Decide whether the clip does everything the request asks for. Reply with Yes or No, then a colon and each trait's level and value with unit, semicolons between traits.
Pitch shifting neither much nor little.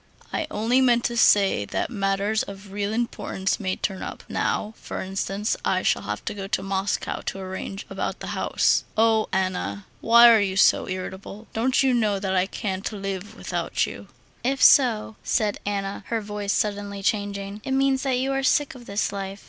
Yes: average, 3.0 semitones